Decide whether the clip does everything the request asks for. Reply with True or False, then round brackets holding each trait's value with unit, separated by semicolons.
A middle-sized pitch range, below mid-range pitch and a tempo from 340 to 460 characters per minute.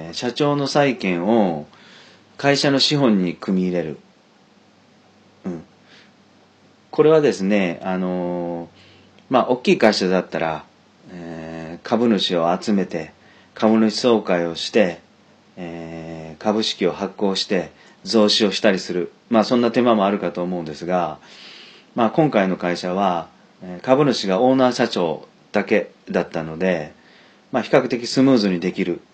False (4.7 semitones; 95 Hz; 255 characters per minute)